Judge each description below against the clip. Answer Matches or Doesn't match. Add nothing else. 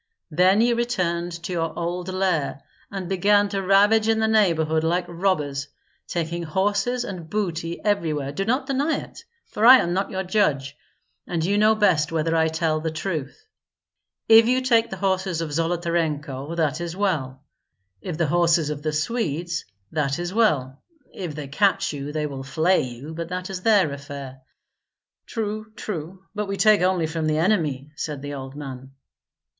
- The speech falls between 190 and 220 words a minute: Doesn't match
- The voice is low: Doesn't match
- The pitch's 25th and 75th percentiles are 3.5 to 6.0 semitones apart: Matches